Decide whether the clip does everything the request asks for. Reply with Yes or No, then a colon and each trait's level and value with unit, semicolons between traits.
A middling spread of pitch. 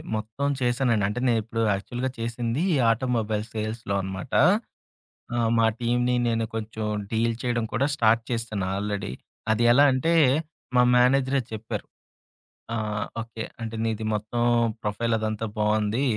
No: narrow, 2.1 semitones